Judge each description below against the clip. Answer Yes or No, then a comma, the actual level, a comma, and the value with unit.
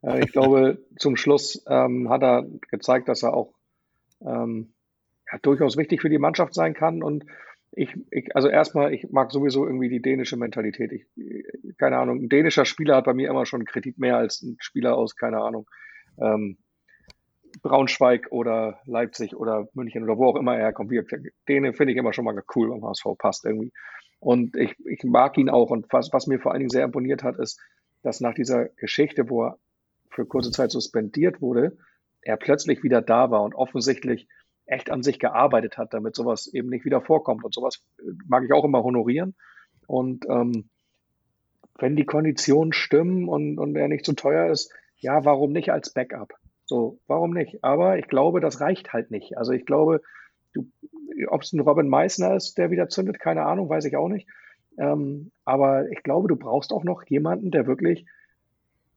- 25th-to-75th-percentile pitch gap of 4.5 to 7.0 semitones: No, average, 3.9 semitones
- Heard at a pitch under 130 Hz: No, low, 135 Hz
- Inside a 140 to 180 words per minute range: No, fast, 190 wpm